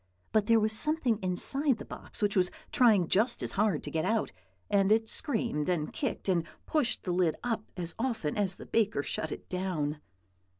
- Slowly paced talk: No, average, 195 wpm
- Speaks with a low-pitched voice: No, high, 205 Hz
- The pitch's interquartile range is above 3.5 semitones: Yes, average, 4.2 semitones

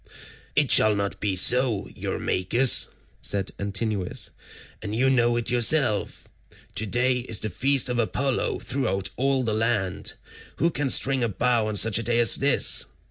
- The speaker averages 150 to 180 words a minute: Yes, average, 155 wpm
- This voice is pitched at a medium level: No, low, 115 Hz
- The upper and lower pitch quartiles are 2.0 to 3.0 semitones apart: No, average, 3.7 semitones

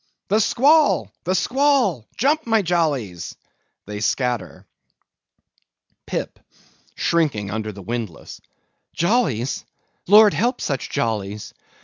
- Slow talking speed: Yes, slow, 95 wpm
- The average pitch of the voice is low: No, medium, 155 Hz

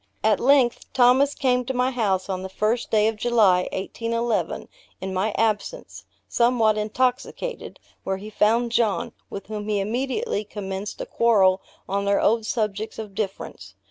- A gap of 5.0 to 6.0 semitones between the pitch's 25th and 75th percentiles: No, average, 3.3 semitones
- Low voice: No, high, 220 Hz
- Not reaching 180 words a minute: Yes, average, 155 wpm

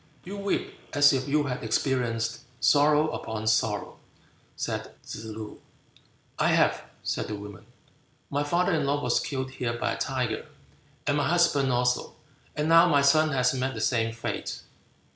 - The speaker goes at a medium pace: Yes, average, 160 wpm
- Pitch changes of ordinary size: Yes, average, 4.2 semitones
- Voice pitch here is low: Yes, low, 130 Hz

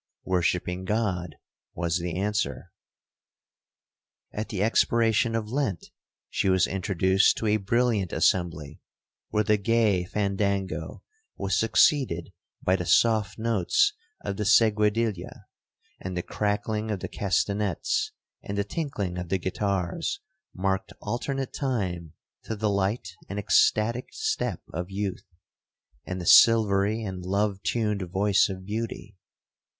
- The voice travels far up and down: No, average, 3.2 semitones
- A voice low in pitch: Yes, low, 100 Hz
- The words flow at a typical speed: No, slow, 125 wpm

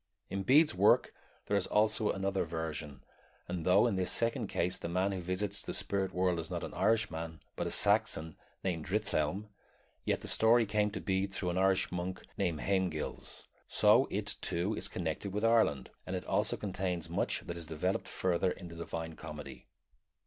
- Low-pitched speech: Yes, very low, 95 Hz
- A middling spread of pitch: Yes, average, 3.4 semitones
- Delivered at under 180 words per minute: No, average, 185 wpm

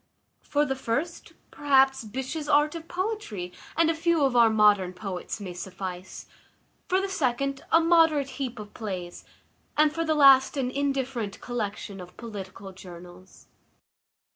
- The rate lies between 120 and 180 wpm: Yes, average, 145 wpm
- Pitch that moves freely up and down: Yes, wide, 7.1 semitones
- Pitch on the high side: Yes, very high, 260 Hz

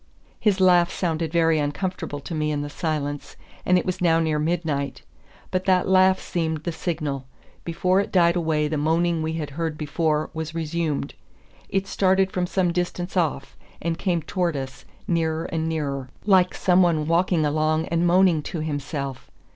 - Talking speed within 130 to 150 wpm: No, average, 170 wpm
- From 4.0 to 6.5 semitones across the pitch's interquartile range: No, average, 2.7 semitones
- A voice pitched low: No, medium, 165 Hz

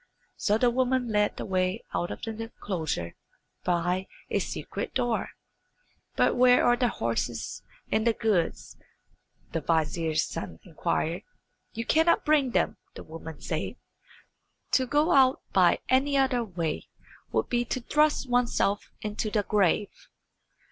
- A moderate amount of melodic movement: No, wide, 6.0 semitones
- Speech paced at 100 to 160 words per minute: Yes, average, 140 wpm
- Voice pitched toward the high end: Yes, high, 220 Hz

